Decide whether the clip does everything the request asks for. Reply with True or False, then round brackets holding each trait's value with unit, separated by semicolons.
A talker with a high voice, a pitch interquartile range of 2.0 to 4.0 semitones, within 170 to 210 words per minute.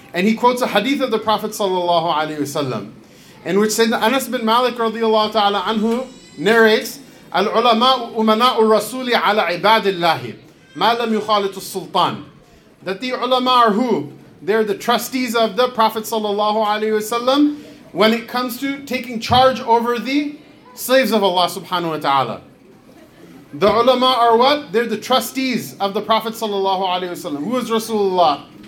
False (225 Hz; 3.6 semitones; 145 wpm)